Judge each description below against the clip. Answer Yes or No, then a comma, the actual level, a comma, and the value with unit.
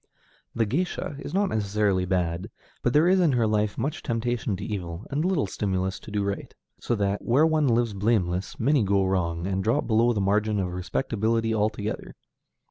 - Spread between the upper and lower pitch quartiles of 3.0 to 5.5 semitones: Yes, average, 3.9 semitones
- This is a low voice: Yes, low, 105 Hz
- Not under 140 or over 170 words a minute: No, average, 185 wpm